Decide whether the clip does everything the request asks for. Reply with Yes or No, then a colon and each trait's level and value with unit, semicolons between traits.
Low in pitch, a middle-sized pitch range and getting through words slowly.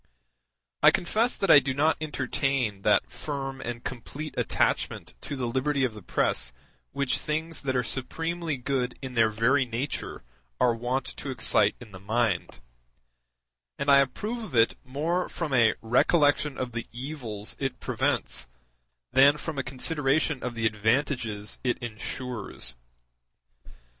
No: low, 130 Hz; average, 3.7 semitones; average, 145 wpm